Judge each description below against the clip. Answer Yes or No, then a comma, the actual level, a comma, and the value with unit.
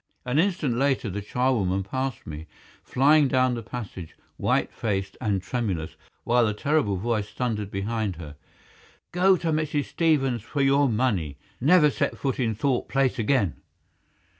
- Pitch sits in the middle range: No, low, 120 Hz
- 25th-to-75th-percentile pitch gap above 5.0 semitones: Yes, wide, 5.4 semitones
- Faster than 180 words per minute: No, average, 150 wpm